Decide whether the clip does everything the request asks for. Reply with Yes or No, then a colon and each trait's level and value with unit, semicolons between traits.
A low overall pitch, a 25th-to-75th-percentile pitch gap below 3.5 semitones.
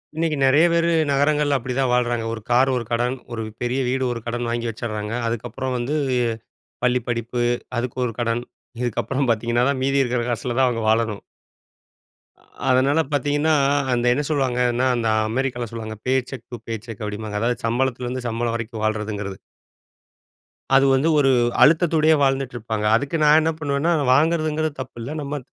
Yes: low, 125 Hz; average, 3.1 semitones